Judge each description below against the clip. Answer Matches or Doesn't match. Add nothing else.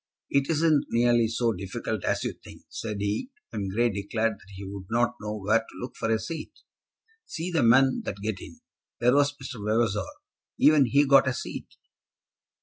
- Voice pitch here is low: Matches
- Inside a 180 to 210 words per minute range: Matches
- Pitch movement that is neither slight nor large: Matches